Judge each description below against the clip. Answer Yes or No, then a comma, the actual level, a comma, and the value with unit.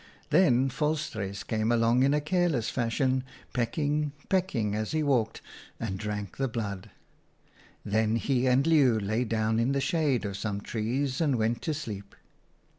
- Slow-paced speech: No, average, 165 wpm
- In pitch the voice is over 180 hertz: No, low, 120 Hz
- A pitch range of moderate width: Yes, average, 4.8 semitones